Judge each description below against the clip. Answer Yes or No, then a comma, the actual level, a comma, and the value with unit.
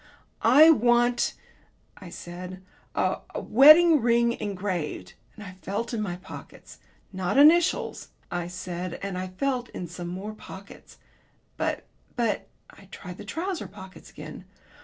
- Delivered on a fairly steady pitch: No, average, 5.0 semitones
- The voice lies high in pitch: Yes, high, 200 Hz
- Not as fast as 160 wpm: Yes, average, 140 wpm